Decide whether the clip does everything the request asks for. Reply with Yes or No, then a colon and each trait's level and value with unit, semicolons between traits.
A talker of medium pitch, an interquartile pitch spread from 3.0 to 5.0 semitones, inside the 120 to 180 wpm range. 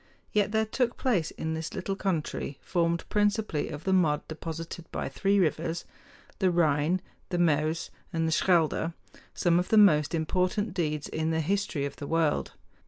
Yes: medium, 170 Hz; average, 3.4 semitones; average, 170 wpm